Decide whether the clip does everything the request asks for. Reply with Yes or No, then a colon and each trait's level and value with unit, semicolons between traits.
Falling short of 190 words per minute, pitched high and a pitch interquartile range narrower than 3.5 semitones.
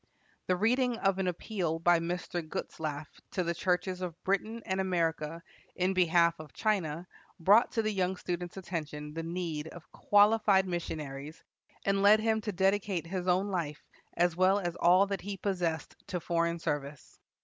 No: average, 165 wpm; medium, 180 Hz; average, 2.9 semitones